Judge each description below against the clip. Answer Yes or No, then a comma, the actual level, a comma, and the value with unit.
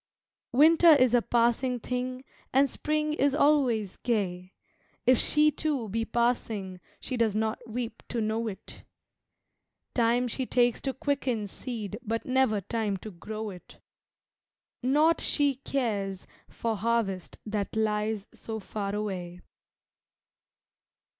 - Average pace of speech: No, slow, 125 wpm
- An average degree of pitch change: Yes, average, 3.5 semitones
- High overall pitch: Yes, high, 230 Hz